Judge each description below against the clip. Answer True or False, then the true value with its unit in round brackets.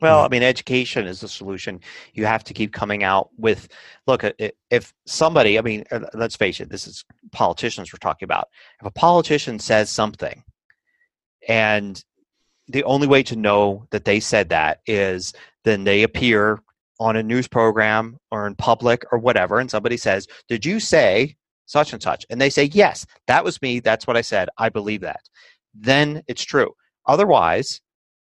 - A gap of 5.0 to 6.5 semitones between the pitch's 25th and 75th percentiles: False (4.1 semitones)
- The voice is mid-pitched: False (115 Hz)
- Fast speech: False (175 wpm)